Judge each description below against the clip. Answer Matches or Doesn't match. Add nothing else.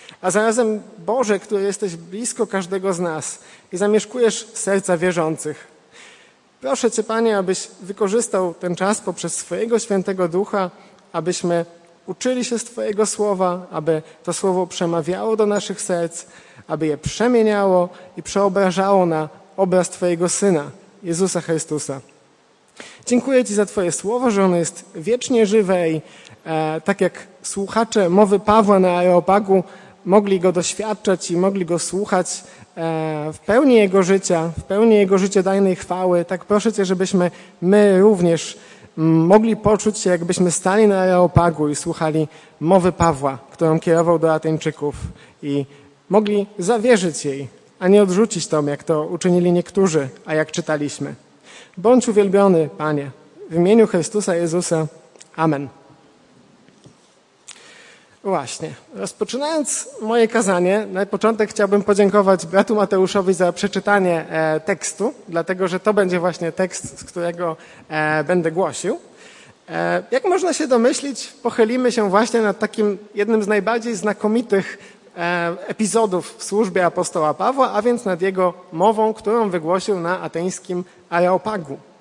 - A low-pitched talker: Doesn't match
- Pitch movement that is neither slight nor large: Matches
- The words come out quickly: Doesn't match